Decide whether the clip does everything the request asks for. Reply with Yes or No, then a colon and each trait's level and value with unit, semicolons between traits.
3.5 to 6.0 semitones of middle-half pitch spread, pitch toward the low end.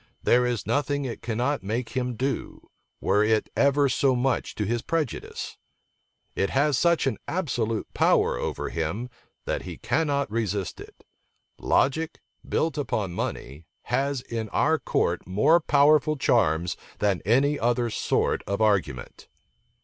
Yes: average, 5.1 semitones; low, 120 Hz